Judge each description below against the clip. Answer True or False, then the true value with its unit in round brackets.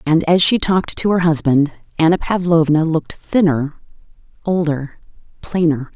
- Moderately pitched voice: True (160 Hz)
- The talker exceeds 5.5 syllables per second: False (4.9 syllables/s)